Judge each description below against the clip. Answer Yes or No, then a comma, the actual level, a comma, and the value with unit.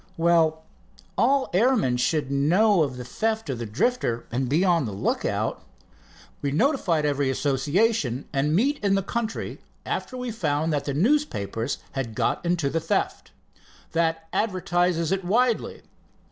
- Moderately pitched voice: Yes, medium, 165 Hz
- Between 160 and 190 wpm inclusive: No, average, 145 wpm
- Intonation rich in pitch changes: Yes, wide, 7.4 semitones